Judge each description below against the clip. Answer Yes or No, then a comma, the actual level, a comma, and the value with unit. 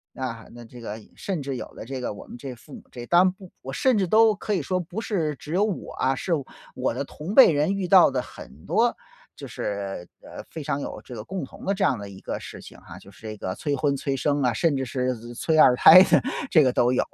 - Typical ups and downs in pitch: No, wide, 6.5 semitones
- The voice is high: No, medium, 140 Hz